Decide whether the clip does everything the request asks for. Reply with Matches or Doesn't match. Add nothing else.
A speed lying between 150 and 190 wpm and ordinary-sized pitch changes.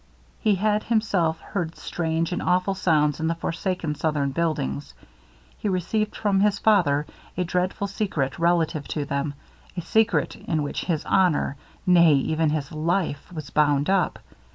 Matches